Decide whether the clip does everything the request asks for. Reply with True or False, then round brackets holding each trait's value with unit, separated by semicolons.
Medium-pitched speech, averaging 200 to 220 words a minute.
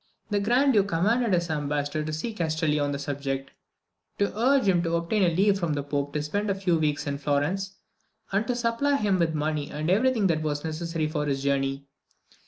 True (165 Hz; 205 wpm)